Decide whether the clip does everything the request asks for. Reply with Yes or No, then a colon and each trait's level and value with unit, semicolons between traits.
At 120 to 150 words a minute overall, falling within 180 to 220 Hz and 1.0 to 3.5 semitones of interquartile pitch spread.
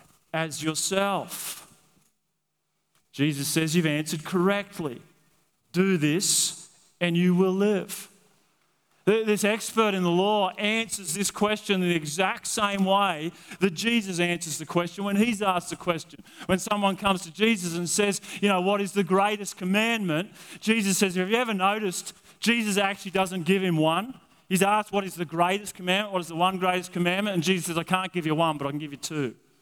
No: average, 180 wpm; high, 190 Hz; average, 2.8 semitones